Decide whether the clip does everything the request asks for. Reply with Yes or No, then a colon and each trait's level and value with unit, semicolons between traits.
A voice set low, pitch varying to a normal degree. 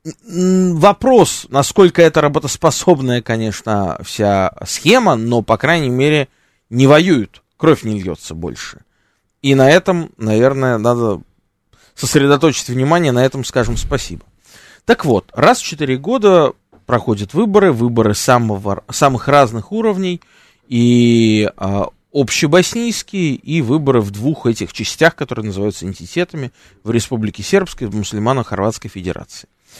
No: low, 125 Hz; wide, 6.7 semitones